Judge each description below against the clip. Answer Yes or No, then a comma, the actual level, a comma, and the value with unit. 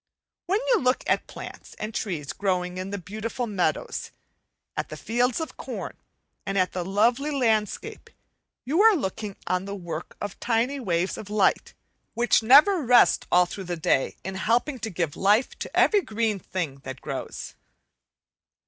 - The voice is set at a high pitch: Yes, high, 210 Hz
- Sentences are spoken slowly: No, average, 165 wpm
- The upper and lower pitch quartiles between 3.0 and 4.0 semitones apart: No, average, 5.0 semitones